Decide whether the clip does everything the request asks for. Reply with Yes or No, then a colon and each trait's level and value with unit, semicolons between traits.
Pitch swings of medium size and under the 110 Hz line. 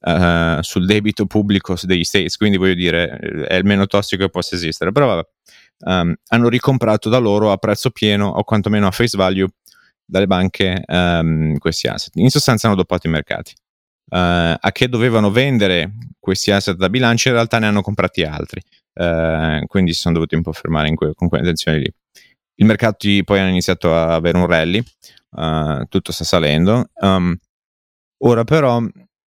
Yes: average, 3.8 semitones; very low, 95 Hz